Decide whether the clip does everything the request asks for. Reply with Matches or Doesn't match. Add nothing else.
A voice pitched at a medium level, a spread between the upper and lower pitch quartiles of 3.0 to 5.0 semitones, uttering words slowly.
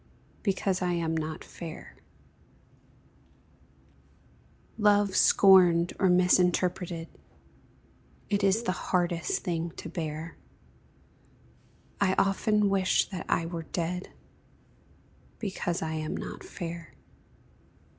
Doesn't match